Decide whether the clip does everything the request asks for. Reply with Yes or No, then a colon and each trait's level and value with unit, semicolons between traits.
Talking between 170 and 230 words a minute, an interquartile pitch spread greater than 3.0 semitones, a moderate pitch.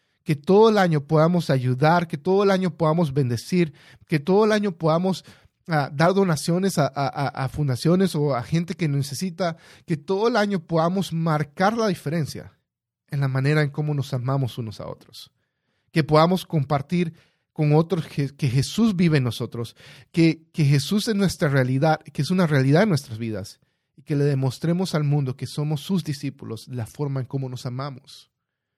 Yes: average, 180 wpm; average, 4.3 semitones; medium, 155 Hz